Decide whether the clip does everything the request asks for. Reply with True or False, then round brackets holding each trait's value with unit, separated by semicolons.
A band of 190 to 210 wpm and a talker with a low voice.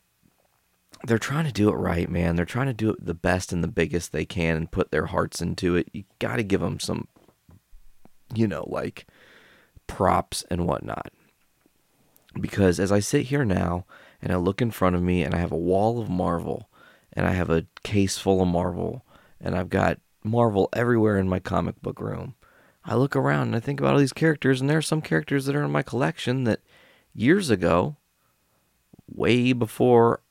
True (200 wpm; 100 Hz)